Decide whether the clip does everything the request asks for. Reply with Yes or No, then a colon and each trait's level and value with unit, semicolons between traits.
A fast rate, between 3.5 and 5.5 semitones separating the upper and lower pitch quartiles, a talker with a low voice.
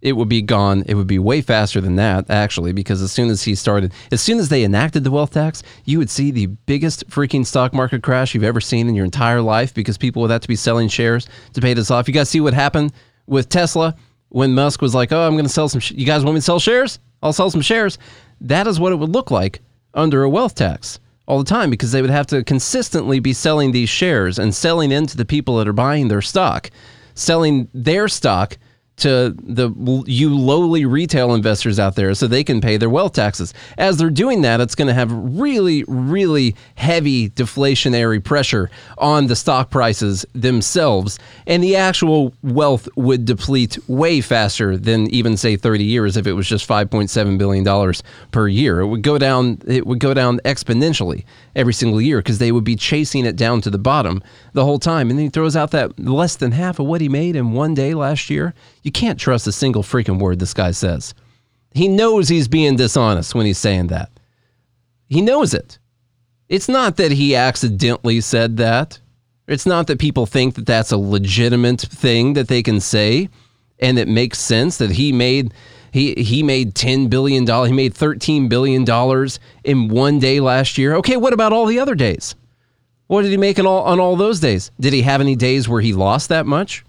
Yes: fast, 215 wpm; average, 4.1 semitones; low, 125 Hz